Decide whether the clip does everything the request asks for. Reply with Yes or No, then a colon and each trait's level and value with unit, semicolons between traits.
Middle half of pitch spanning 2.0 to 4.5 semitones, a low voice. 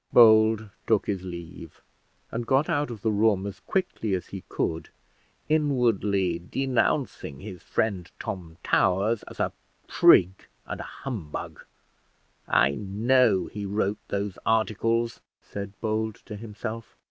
Yes: average, 3.2 semitones; low, 105 Hz